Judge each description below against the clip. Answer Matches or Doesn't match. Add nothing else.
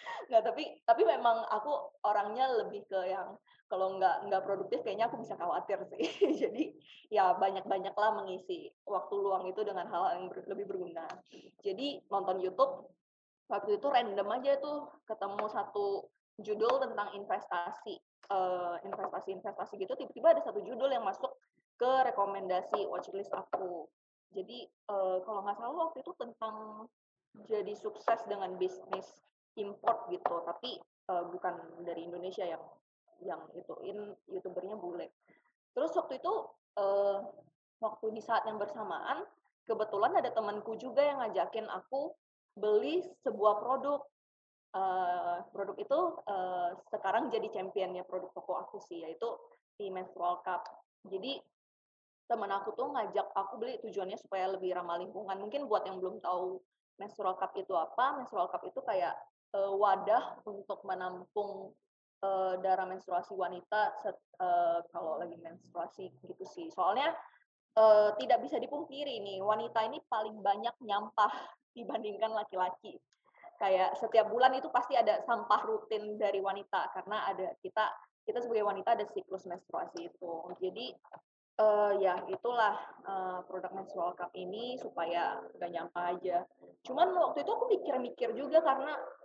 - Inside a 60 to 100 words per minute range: Doesn't match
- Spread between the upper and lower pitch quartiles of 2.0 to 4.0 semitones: Doesn't match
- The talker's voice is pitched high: Matches